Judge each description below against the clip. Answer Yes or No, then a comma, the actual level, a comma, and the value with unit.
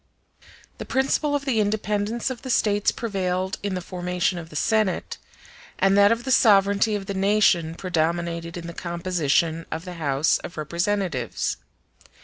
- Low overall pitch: No, medium, 185 Hz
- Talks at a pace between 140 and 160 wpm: Yes, average, 155 wpm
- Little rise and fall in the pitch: No, average, 3.6 semitones